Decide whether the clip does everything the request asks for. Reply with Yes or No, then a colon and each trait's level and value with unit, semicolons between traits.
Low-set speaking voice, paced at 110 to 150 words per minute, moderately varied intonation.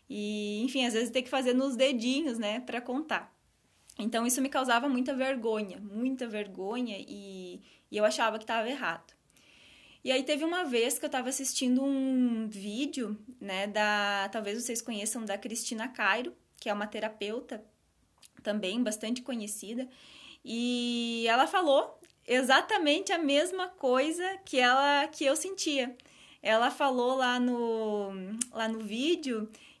No: high, 245 Hz; average, 145 wpm; average, 3.6 semitones